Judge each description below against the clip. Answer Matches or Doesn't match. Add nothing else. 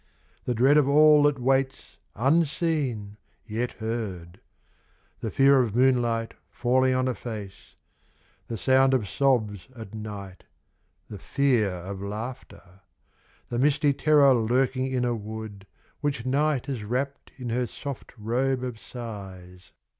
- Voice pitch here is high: Doesn't match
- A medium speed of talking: Doesn't match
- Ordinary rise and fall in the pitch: Matches